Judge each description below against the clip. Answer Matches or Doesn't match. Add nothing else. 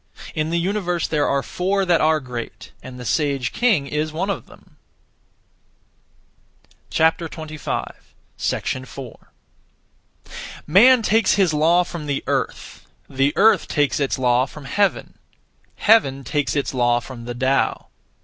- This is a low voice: Doesn't match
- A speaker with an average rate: Doesn't match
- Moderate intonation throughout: Matches